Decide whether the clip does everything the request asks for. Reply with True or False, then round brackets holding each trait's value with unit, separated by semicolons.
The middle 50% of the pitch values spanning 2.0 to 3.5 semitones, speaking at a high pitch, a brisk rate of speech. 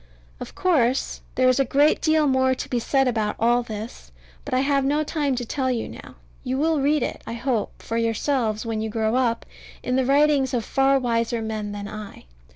True (3.2 semitones; 255 Hz; 210 wpm)